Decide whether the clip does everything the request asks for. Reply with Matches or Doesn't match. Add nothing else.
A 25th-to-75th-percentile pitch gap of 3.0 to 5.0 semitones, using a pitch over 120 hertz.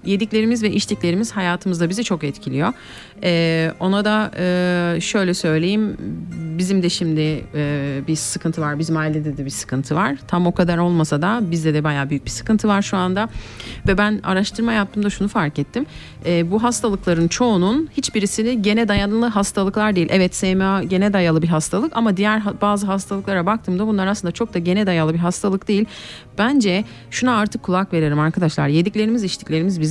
Matches